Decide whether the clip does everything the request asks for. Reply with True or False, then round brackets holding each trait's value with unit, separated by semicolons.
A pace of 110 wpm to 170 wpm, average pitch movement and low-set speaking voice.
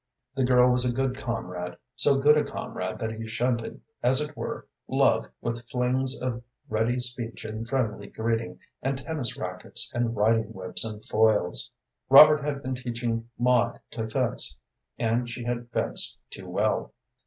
False (160 wpm; 2.3 semitones; 120 Hz)